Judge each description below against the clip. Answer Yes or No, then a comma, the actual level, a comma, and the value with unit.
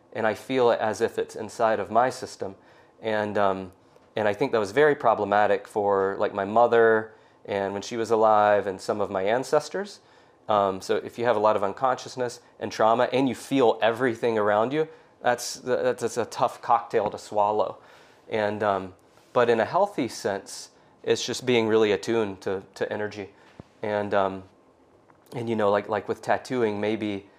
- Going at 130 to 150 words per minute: No, average, 180 wpm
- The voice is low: Yes, low, 105 Hz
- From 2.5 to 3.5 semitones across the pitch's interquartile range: Yes, average, 3.1 semitones